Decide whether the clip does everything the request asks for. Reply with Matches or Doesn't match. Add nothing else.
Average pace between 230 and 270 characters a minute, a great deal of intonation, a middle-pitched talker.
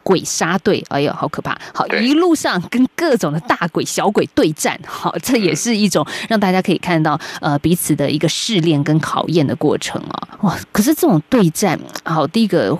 Doesn't match